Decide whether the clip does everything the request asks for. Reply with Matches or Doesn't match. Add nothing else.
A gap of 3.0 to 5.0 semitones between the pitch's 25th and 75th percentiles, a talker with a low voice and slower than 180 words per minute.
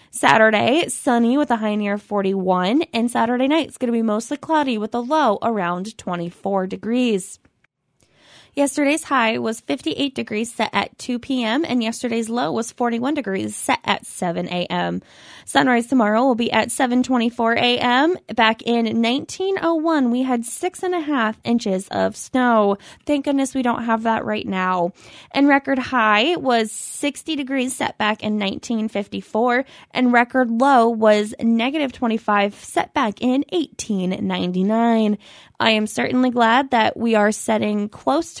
Doesn't match